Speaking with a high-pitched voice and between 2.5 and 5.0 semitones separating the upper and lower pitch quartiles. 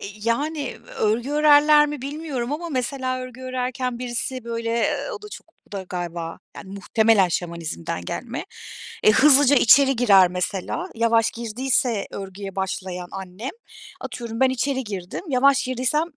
No: high, 240 Hz; wide, 5.4 semitones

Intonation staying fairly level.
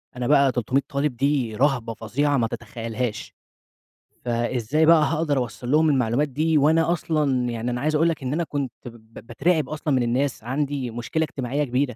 No: average, 3.8 semitones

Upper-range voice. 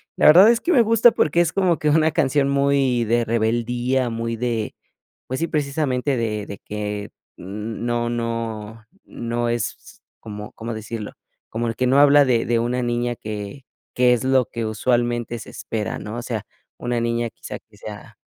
No: low, 120 Hz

